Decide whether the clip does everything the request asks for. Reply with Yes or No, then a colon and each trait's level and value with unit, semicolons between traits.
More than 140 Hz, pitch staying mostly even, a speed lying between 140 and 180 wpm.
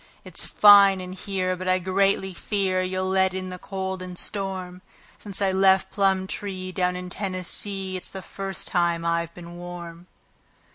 Yes: medium, 185 Hz; narrow, 1.1 semitones; average, 160 wpm